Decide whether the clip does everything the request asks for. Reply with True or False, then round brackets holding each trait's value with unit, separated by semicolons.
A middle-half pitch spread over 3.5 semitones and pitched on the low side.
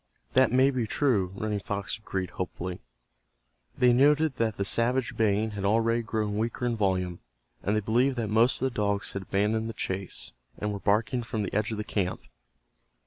False (2.9 semitones; 110 Hz)